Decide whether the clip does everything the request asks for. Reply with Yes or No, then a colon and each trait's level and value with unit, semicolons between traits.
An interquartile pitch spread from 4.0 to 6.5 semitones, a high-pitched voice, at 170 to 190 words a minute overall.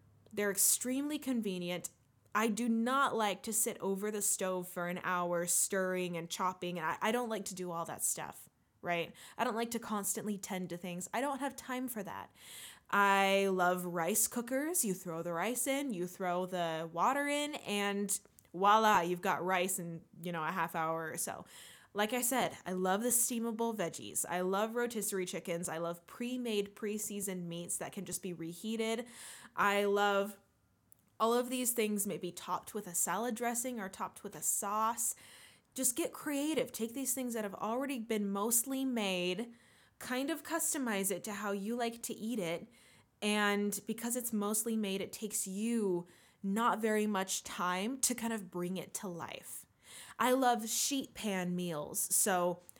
Yes: average, 4.6 semitones; high, 205 Hz; average, 175 wpm